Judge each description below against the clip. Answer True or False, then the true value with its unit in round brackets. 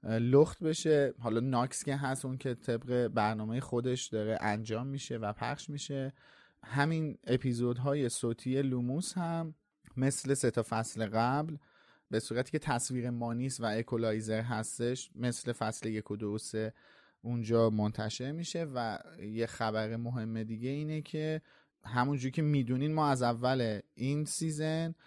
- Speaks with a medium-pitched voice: False (125 Hz)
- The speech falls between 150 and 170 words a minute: False (140 wpm)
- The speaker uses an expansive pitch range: False (4.0 semitones)